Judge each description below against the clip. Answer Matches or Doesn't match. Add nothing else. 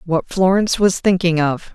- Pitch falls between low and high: Matches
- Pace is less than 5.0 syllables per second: Doesn't match